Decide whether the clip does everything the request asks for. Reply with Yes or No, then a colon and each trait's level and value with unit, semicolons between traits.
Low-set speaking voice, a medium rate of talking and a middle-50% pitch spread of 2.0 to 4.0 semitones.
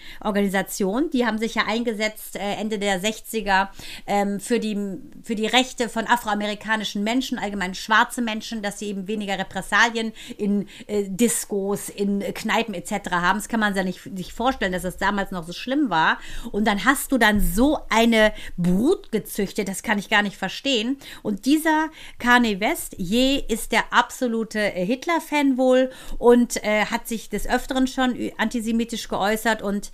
No: high, 220 Hz; average, 170 wpm; average, 3.2 semitones